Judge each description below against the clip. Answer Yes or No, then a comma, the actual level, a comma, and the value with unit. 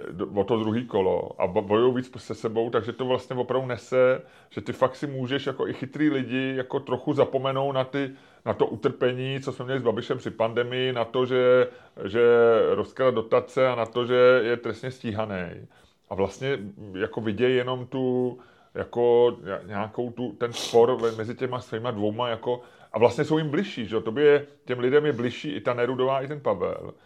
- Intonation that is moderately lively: No, narrow, 2.2 semitones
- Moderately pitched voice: No, low, 125 Hz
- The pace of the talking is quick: Yes, fast, 190 wpm